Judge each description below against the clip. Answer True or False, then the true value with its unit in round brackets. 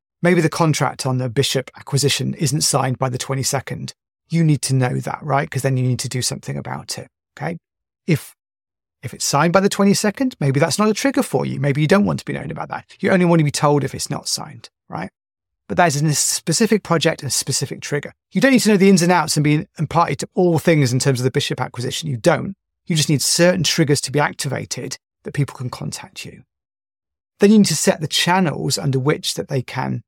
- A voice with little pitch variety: False (4.7 semitones)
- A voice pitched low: False (150 Hz)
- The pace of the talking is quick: True (245 wpm)